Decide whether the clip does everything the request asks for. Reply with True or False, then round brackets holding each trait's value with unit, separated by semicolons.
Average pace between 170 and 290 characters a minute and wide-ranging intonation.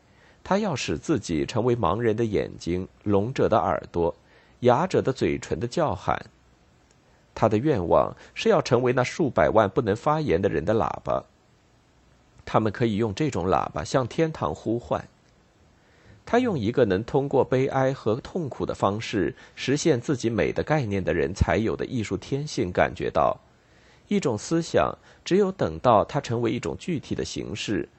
True (240 characters per minute; 6.4 semitones)